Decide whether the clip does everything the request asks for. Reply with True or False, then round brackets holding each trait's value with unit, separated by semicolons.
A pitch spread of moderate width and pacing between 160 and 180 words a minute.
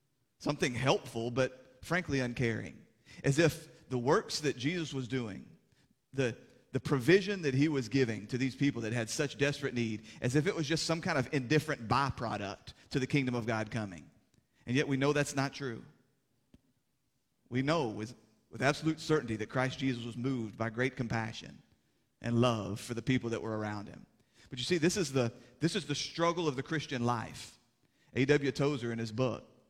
False (3.7 semitones; 190 wpm)